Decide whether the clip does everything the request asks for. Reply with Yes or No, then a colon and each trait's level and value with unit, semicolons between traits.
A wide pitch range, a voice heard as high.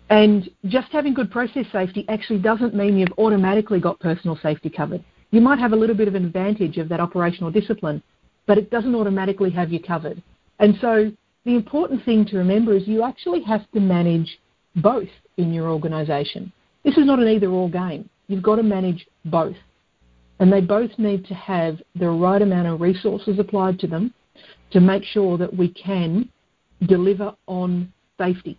No: average, 3.5 semitones; high, 195 Hz